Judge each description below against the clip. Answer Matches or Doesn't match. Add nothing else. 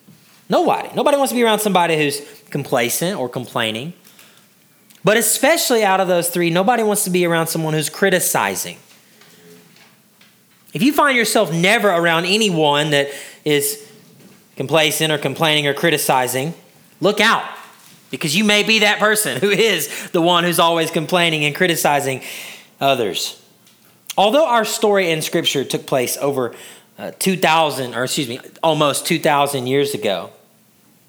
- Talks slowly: Doesn't match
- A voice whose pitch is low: Doesn't match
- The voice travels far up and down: Matches